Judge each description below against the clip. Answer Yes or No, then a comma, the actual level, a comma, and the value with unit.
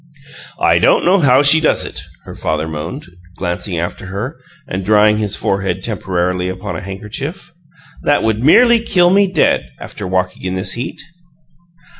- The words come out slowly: No, average, 160 wpm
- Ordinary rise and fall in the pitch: No, wide, 7.9 semitones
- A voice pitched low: Yes, low, 105 Hz